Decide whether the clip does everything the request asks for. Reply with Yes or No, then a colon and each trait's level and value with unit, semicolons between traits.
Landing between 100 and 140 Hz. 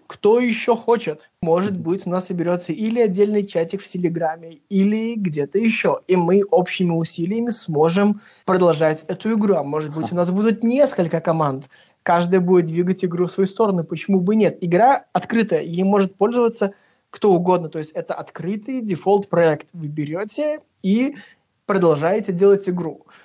No: medium, 185 Hz